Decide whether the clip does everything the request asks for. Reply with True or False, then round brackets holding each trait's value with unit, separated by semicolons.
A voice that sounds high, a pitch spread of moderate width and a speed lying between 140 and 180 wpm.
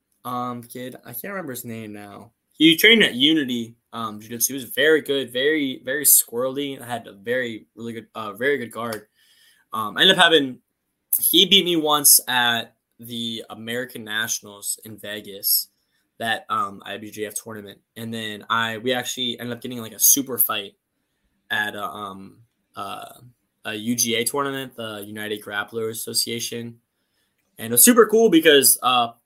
False (120 Hz; 3.5 semitones; 165 wpm)